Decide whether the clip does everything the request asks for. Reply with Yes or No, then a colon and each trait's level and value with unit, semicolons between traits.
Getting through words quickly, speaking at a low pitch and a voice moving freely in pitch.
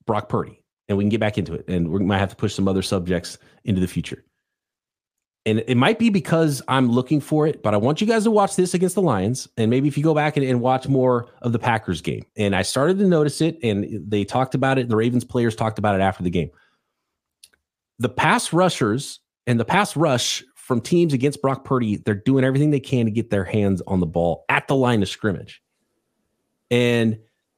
Yes: fast, 230 wpm; low, 120 Hz; wide, 5.8 semitones